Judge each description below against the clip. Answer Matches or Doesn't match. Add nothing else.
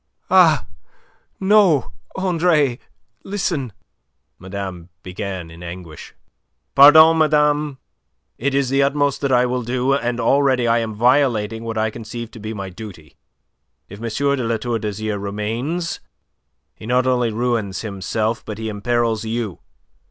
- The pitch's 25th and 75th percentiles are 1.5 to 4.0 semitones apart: Doesn't match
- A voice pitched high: Doesn't match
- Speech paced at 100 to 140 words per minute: Matches